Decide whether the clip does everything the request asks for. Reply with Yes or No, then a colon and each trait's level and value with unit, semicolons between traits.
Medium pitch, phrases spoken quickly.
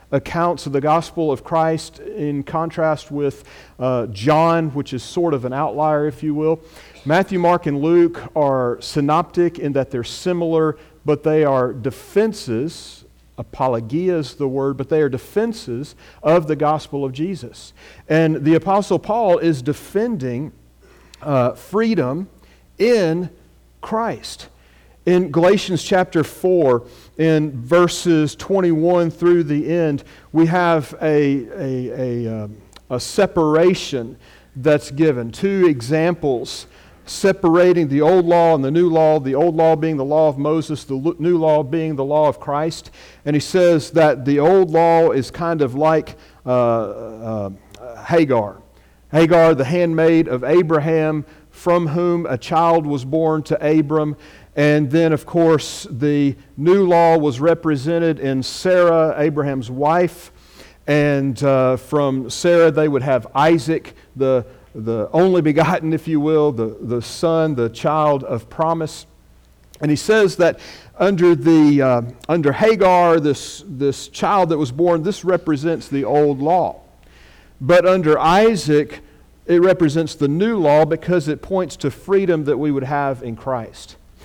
No: medium, 155 Hz; average, 145 wpm